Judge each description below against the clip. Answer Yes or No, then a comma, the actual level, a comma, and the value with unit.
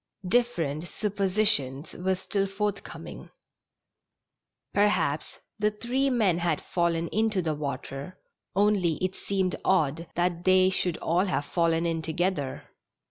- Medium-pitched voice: Yes, medium, 180 Hz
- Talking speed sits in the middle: No, slow, 125 wpm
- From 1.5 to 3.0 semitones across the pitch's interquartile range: No, average, 3.6 semitones